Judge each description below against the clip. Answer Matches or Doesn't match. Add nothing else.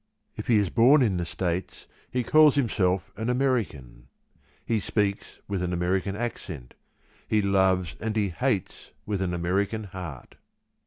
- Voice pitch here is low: Matches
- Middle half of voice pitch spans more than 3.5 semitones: Matches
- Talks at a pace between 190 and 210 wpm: Doesn't match